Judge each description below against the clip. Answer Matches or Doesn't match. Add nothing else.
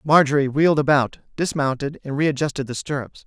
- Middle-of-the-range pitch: Matches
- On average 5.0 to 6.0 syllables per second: Matches